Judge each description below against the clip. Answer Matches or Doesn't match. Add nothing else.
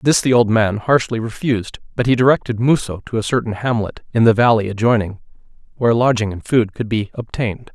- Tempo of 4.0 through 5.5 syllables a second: Doesn't match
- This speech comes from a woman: Doesn't match